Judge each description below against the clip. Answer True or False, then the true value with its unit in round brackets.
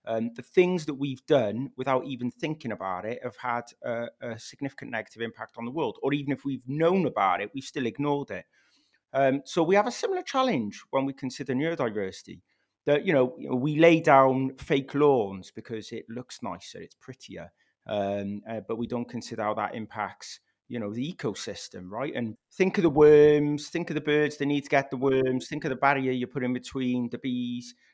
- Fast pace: True (210 wpm)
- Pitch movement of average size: True (4.0 semitones)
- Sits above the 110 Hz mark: True (135 Hz)